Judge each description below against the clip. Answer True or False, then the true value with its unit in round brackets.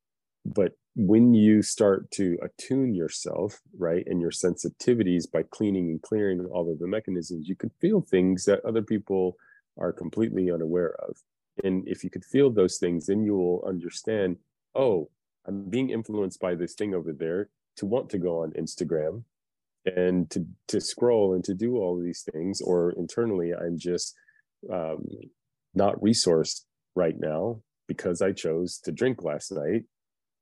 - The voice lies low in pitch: True (95 Hz)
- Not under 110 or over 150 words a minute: False (165 wpm)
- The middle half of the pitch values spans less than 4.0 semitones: True (3.5 semitones)